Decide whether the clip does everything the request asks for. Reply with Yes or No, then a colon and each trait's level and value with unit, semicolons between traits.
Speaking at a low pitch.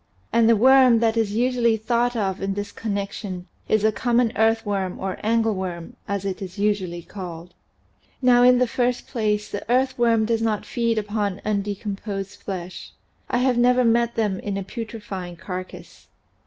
No: high, 215 Hz